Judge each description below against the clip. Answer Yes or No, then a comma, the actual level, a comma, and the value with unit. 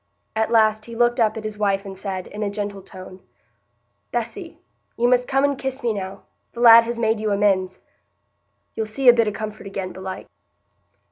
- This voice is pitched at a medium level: No, high, 215 Hz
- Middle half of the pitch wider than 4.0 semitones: No, average, 2.9 semitones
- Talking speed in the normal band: Yes, average, 190 wpm